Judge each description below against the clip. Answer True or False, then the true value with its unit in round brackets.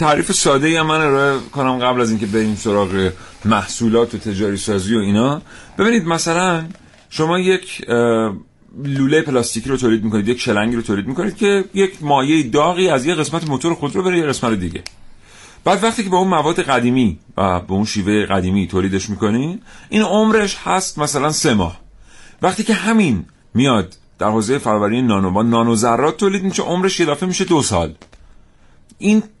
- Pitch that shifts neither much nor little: False (8.9 semitones)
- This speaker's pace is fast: True (170 wpm)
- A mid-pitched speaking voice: False (130 Hz)